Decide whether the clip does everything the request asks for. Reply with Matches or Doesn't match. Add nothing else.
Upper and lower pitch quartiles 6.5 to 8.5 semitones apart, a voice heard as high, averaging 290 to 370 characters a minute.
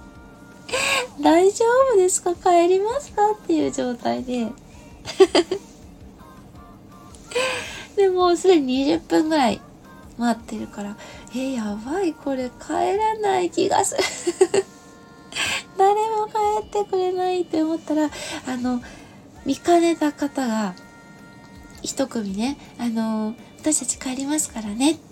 Doesn't match